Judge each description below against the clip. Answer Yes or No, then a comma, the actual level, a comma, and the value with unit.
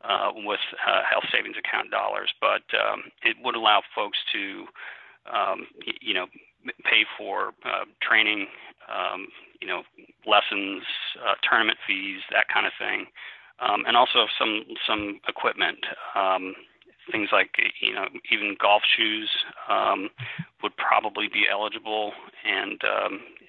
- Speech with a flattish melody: Yes, narrow, 1.5 semitones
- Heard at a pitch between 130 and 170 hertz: No, low, 105 Hz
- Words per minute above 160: No, slow, 135 wpm